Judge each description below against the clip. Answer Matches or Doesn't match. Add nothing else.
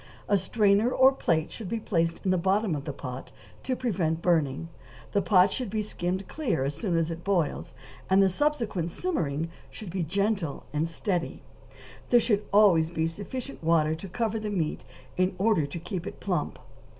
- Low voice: Doesn't match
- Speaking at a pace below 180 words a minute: Doesn't match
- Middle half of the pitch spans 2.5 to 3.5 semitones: Doesn't match